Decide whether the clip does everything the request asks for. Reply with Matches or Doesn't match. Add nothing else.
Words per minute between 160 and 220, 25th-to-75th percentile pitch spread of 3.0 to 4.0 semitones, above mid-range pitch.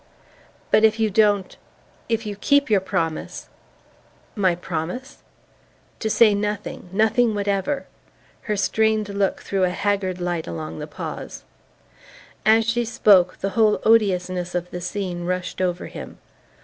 Doesn't match